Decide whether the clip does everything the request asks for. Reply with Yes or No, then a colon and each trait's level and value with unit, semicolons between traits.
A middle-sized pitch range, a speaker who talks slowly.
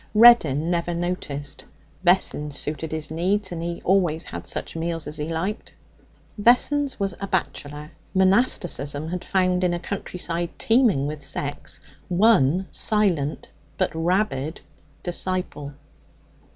Yes: average, 4.0 semitones; slow, 125 wpm